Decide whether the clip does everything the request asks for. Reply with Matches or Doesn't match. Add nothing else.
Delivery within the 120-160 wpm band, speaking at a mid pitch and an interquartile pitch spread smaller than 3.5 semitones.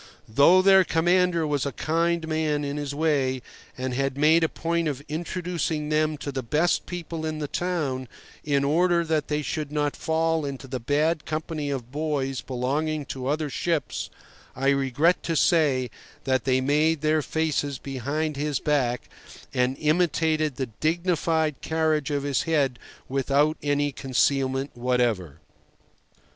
Matches